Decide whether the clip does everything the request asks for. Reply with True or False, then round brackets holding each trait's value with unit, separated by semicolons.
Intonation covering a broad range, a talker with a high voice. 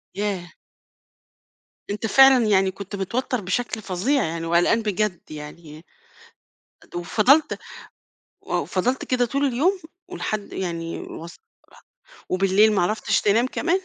True (5.7 semitones; 205 Hz)